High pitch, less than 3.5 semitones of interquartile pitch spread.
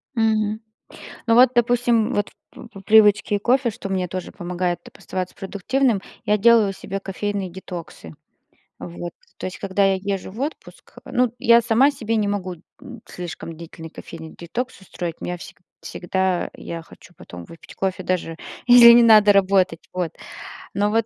No: high, 200 Hz; average, 4.1 semitones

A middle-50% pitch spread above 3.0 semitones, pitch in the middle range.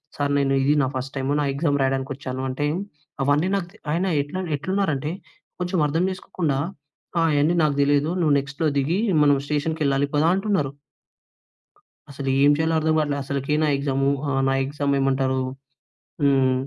No: narrow, 2.6 semitones; medium, 145 Hz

